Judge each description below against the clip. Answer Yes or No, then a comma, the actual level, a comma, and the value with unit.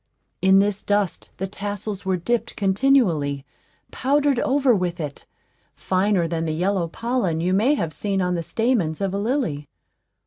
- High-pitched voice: Yes, high, 195 Hz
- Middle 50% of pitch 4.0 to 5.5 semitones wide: Yes, average, 4.9 semitones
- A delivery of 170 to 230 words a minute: No, average, 160 wpm